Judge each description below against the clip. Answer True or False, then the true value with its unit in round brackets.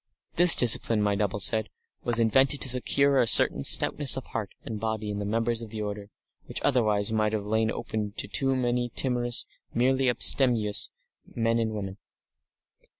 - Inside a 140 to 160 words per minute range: False (170 wpm)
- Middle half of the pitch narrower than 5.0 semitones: True (2.8 semitones)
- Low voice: True (115 Hz)